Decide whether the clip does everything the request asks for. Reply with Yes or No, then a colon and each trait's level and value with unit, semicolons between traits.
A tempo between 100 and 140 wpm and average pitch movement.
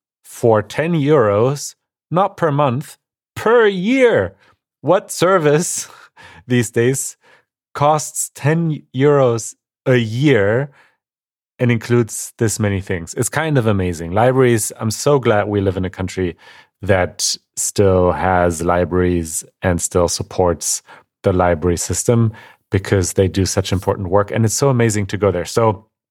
No: slow, 135 wpm; wide, 6.4 semitones